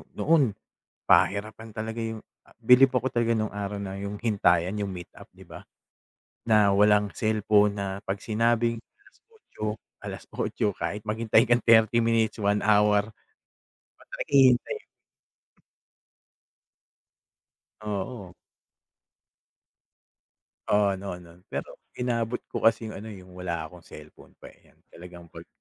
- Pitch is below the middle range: Yes, low, 105 Hz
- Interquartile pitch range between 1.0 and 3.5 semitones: Yes, narrow, 2.4 semitones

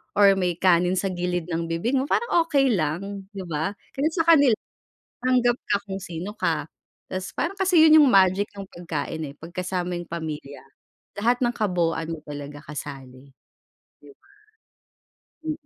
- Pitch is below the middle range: No, medium, 185 Hz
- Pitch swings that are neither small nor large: No, wide, 6.5 semitones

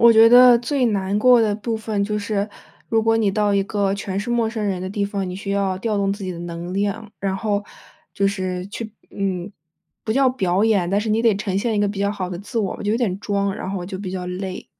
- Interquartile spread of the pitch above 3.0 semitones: No, narrow, 2.4 semitones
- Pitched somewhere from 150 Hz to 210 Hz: Yes, high, 200 Hz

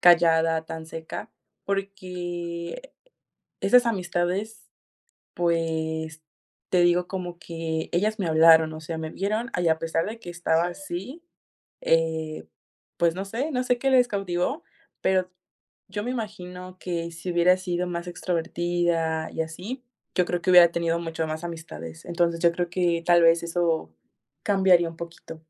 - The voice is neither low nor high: Yes, medium, 175 Hz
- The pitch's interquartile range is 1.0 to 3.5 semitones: Yes, narrow, 2.4 semitones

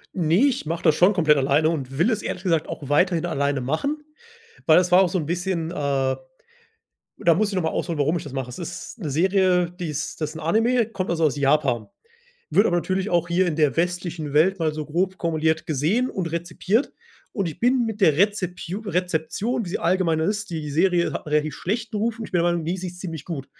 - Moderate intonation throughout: Yes, average, 3.5 semitones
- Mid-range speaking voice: Yes, medium, 170 Hz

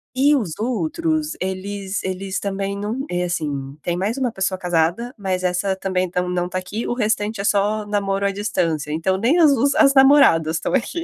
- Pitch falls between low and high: No, high, 195 Hz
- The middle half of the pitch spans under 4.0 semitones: No, average, 4.5 semitones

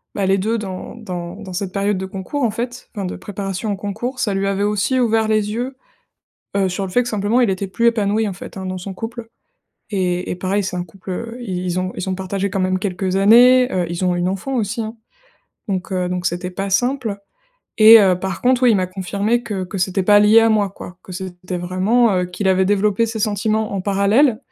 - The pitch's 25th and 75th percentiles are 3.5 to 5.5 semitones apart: No, average, 3.0 semitones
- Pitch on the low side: No, high, 200 Hz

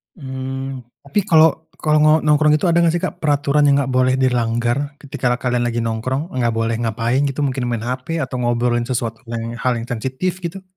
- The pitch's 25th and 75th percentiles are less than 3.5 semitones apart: No, average, 3.8 semitones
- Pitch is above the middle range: No, low, 130 Hz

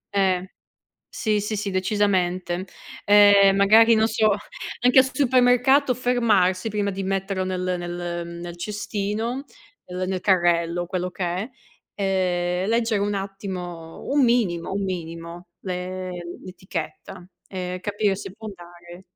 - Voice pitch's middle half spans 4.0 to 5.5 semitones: No, average, 2.8 semitones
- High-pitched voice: Yes, high, 195 Hz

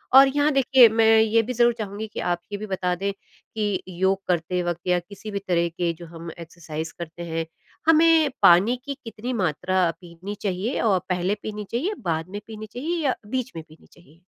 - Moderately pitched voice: No, high, 195 Hz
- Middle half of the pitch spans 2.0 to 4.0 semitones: No, average, 4.8 semitones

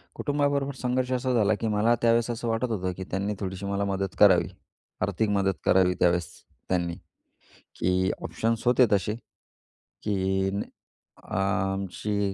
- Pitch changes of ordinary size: Yes, average, 3.5 semitones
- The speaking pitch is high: No, low, 100 Hz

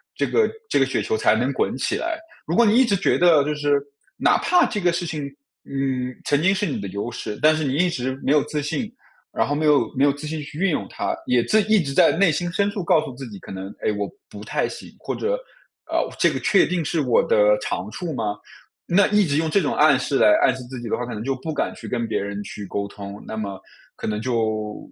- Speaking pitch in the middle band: Yes, medium, 145 Hz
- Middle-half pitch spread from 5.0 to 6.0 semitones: No, wide, 7.1 semitones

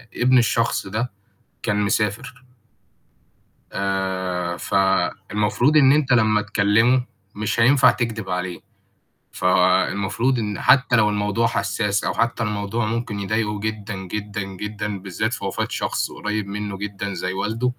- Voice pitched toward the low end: Yes, low, 105 Hz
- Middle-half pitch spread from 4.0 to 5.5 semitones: No, average, 2.8 semitones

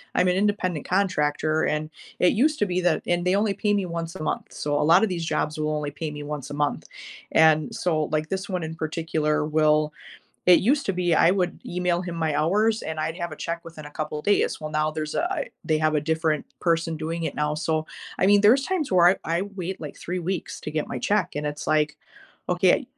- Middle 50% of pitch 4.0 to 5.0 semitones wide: No, average, 3.1 semitones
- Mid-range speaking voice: Yes, medium, 165 Hz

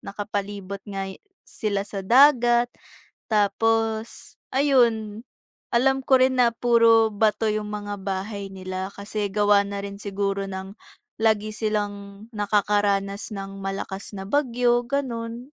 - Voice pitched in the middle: No, high, 210 Hz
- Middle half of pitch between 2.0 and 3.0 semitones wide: Yes, narrow, 2.6 semitones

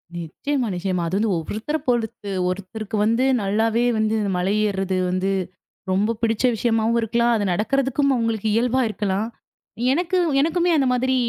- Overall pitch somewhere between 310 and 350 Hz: No, high, 220 Hz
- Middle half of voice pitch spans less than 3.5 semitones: No, average, 3.8 semitones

